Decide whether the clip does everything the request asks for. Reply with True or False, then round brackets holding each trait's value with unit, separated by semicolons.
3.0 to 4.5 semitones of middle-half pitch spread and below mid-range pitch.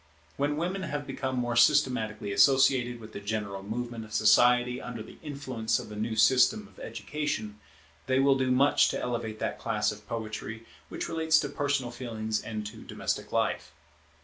True (3.9 semitones; 120 Hz)